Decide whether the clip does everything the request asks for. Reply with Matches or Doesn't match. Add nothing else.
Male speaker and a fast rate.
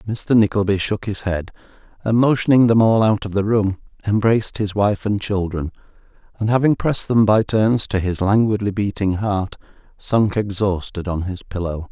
Doesn't match